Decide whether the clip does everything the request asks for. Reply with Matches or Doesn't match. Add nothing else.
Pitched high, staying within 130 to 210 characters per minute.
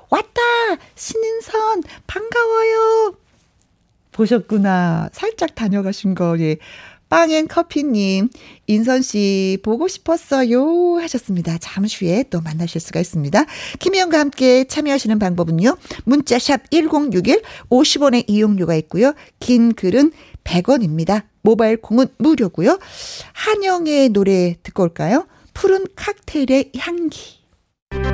Doesn't match